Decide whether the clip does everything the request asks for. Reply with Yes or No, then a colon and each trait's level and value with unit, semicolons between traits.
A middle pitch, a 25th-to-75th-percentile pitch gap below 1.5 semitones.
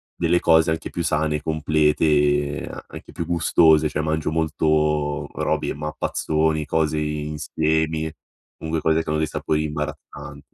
No: very low, 75 Hz; narrow, 0.9 semitones